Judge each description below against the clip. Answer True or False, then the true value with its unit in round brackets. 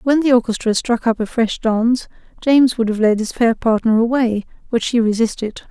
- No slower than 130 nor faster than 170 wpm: False (200 wpm)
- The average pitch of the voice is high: True (230 Hz)